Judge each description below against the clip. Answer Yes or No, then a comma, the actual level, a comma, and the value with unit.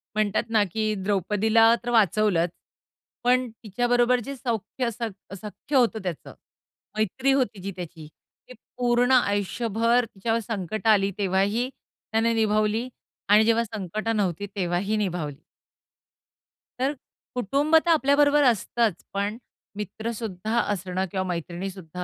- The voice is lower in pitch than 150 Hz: No, high, 215 Hz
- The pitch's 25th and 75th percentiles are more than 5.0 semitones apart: No, average, 3.5 semitones